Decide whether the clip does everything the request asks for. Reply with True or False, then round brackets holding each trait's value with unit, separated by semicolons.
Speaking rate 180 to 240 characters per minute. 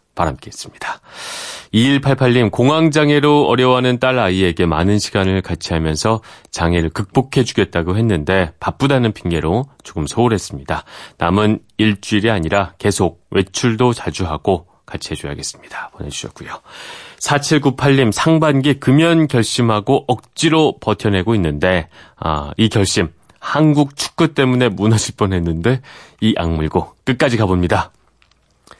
False (295 characters per minute)